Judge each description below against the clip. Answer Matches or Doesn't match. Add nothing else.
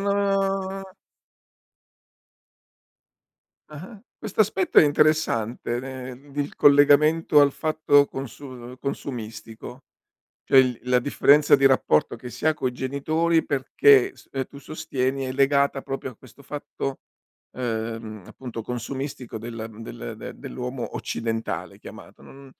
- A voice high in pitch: Doesn't match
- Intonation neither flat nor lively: Matches